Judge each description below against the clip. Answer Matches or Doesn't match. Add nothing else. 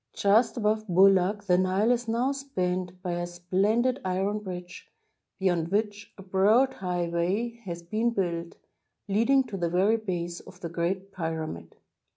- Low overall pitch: Doesn't match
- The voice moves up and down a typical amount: Matches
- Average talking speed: Matches